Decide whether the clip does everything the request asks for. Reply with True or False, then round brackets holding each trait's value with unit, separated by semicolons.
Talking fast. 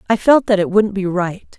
True (265 wpm)